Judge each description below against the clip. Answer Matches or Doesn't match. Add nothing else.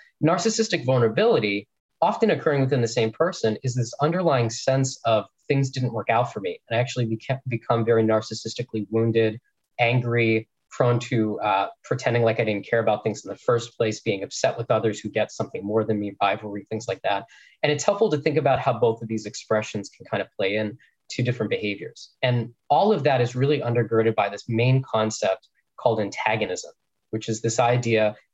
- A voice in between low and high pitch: Doesn't match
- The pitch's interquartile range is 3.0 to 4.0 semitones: Matches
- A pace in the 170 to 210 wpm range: Matches